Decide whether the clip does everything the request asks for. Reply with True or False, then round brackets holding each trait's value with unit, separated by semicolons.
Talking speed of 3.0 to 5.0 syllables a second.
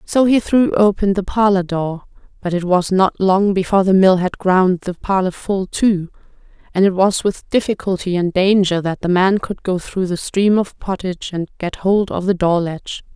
True (4.8 syllables/s)